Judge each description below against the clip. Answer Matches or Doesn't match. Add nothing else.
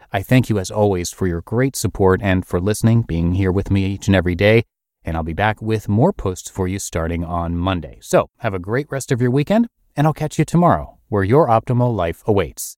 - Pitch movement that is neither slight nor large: Matches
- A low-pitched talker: Matches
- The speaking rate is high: Matches